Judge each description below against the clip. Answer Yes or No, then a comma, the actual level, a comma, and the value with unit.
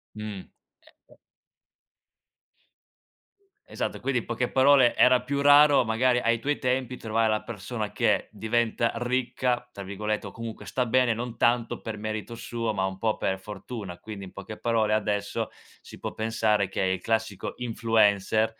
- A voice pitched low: Yes, low, 115 Hz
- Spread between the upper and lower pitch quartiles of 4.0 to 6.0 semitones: No, narrow, 2.5 semitones